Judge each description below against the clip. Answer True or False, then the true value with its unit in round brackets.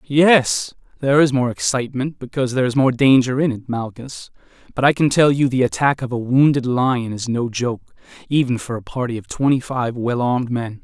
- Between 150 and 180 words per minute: False (205 wpm)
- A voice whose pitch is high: False (130 Hz)